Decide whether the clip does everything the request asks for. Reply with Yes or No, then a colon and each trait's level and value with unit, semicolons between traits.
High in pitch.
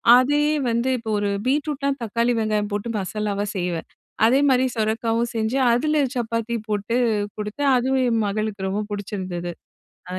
Yes: high, 225 Hz